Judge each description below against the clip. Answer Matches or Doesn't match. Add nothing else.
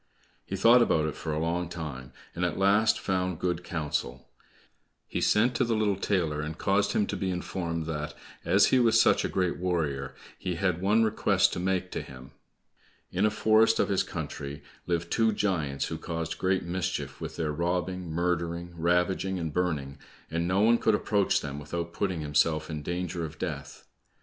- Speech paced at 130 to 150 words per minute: Doesn't match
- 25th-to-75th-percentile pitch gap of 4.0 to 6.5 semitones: Doesn't match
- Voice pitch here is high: Doesn't match